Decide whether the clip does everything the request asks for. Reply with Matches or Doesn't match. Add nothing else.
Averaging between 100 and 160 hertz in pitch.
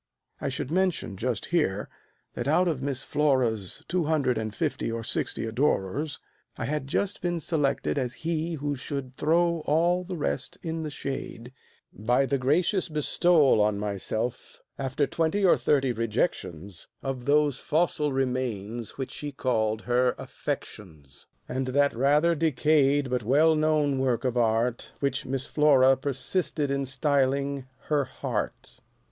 Matches